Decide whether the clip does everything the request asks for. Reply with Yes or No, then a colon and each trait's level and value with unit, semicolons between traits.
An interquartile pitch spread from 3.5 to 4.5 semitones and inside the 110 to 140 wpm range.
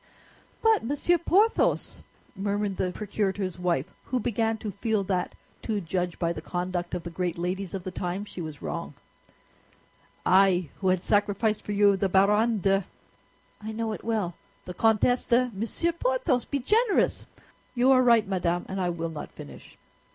No: average, 4.0 semitones; average, 165 wpm